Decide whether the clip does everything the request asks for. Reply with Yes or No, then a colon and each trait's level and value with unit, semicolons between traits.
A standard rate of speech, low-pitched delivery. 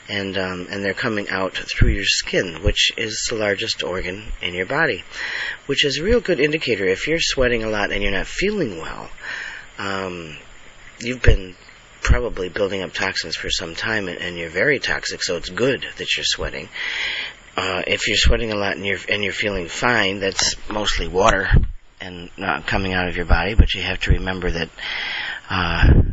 No: fast, 215 wpm; very low, 95 Hz